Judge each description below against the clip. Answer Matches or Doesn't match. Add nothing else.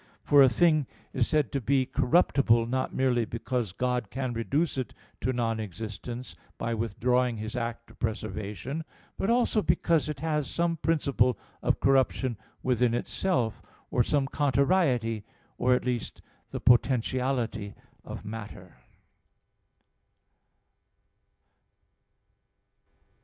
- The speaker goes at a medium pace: Doesn't match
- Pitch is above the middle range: Doesn't match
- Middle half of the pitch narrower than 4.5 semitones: Matches